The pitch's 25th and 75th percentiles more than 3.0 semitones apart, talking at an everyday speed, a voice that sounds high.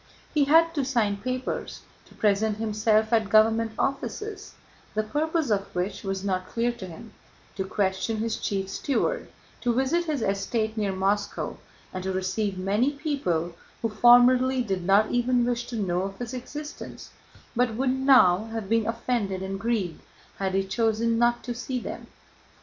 Yes: average, 4.2 semitones; average, 165 wpm; high, 225 Hz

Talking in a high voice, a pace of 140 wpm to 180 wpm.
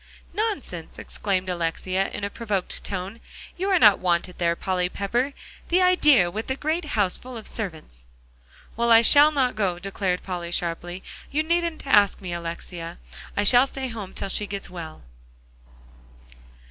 Yes: high, 200 Hz; average, 160 wpm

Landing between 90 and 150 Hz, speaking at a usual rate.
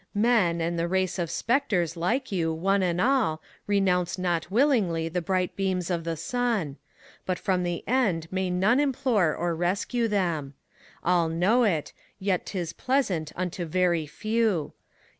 No: medium, 180 Hz; average, 160 wpm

